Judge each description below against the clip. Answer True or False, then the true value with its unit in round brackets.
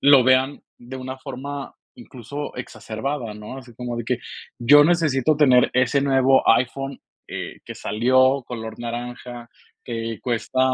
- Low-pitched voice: True (130 Hz)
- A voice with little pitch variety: True (2.3 semitones)